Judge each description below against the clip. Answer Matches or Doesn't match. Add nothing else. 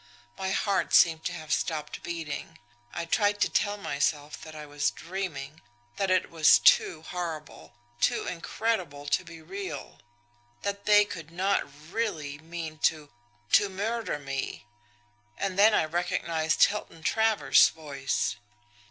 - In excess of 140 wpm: Doesn't match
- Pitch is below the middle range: Doesn't match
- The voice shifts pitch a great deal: Doesn't match